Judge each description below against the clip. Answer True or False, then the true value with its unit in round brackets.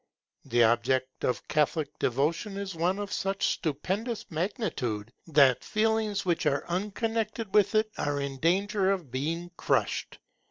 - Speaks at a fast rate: False (135 wpm)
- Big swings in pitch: True (6.5 semitones)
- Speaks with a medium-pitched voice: True (175 Hz)